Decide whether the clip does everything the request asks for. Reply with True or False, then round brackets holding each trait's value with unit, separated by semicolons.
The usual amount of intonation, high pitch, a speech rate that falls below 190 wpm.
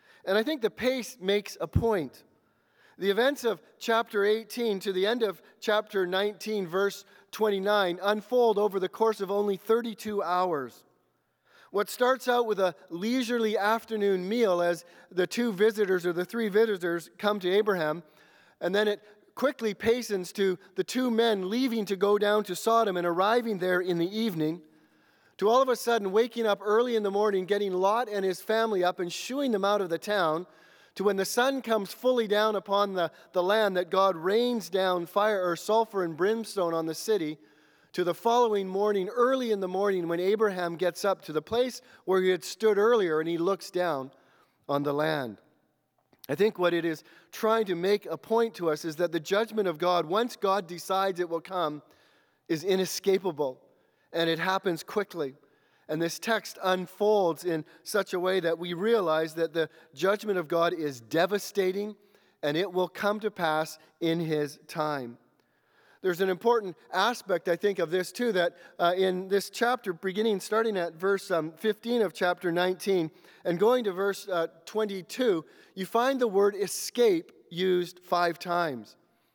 True (3.8 semitones; 195 Hz; 180 wpm)